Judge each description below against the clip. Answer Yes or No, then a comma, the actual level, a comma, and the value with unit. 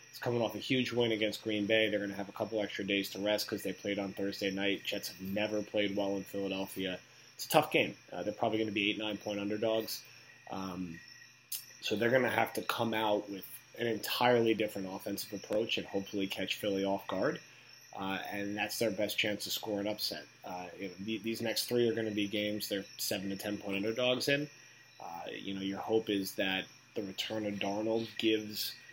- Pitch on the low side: Yes, low, 105 Hz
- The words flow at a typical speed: No, fast, 220 wpm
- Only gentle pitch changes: Yes, narrow, 2.0 semitones